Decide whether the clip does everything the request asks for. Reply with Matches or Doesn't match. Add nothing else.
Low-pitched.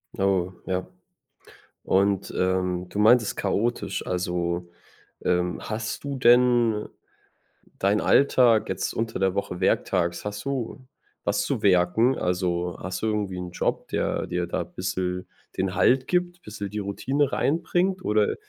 Matches